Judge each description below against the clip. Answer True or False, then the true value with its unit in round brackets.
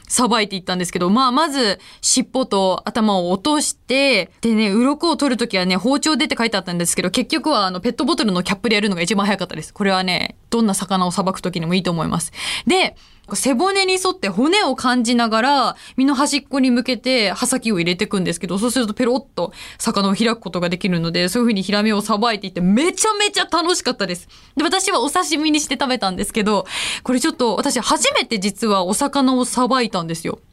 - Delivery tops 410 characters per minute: True (445 characters per minute)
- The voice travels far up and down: True (6.0 semitones)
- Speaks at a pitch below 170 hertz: False (230 Hz)